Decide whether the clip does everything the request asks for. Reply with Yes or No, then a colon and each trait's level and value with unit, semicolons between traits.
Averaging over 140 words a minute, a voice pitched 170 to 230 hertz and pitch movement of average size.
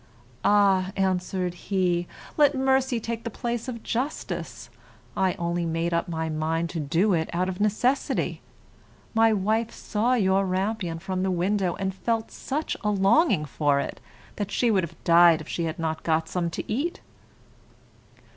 Yes: average, 165 wpm; high, 190 Hz; average, 4.7 semitones